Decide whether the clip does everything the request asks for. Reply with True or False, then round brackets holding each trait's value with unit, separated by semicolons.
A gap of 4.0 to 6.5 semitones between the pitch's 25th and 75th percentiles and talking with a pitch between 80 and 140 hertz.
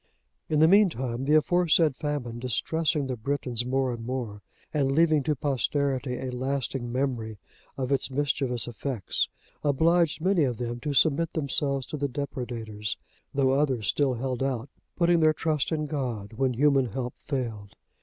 False (3.3 semitones; 135 Hz)